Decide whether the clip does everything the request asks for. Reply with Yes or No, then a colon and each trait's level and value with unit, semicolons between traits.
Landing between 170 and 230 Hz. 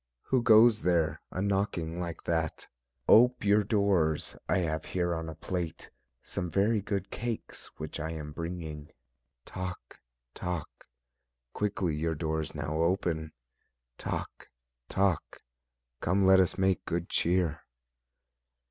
No: very low, 90 Hz